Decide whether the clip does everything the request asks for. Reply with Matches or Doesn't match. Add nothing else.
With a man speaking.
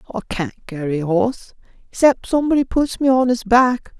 Matches